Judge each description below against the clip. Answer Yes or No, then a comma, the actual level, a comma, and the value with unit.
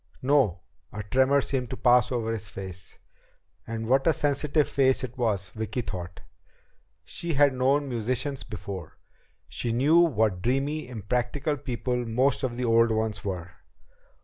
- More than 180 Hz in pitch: No, low, 125 Hz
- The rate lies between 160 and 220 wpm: No, average, 150 wpm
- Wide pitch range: No, average, 3.7 semitones